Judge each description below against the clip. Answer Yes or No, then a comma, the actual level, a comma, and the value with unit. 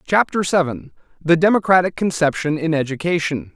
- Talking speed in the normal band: No, slow, 120 wpm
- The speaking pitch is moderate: Yes, medium, 165 Hz